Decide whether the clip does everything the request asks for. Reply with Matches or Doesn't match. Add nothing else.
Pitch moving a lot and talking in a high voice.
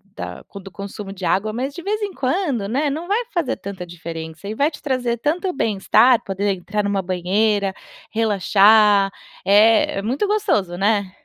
Matches